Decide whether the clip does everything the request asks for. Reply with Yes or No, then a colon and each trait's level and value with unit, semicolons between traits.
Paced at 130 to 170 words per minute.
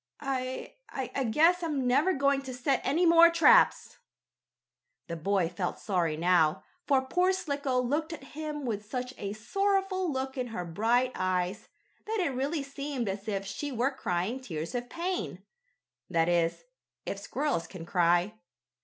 Yes: average, 155 wpm